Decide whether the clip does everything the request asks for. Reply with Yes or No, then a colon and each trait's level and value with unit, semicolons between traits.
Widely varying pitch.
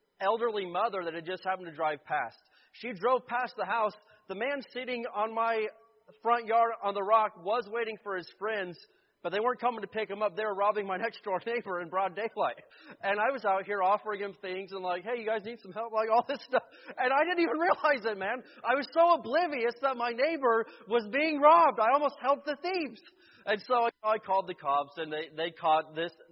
No: average, 4.1 semitones